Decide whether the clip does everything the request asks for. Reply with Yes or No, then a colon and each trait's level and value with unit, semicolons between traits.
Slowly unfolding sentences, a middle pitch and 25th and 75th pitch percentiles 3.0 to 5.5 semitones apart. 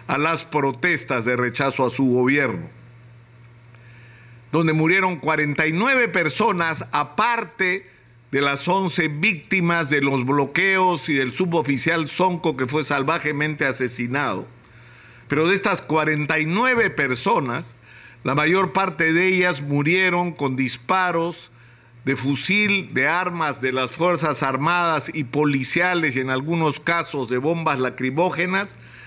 Yes: slow, 120 wpm; medium, 150 Hz; average, 5.2 semitones